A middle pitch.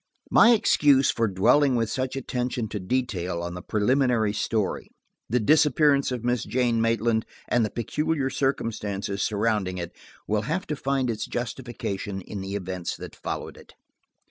No: low, 115 Hz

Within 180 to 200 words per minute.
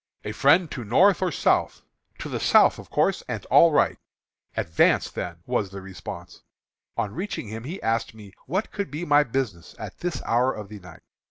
Yes: average, 190 wpm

